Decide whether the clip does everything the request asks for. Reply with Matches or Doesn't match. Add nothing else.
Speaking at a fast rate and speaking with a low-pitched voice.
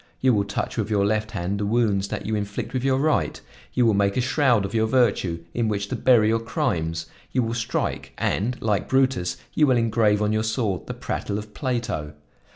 Matches